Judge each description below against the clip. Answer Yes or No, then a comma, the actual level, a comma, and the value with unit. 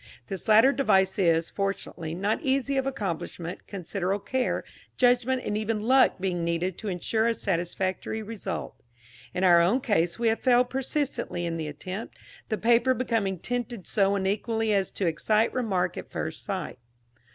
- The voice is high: Yes, high, 205 Hz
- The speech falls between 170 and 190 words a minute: No, average, 160 wpm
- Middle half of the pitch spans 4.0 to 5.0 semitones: Yes, average, 4.7 semitones